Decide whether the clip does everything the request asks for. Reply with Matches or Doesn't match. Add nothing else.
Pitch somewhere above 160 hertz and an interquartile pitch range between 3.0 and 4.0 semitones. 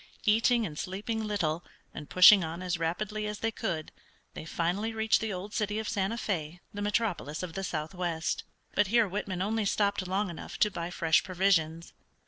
Matches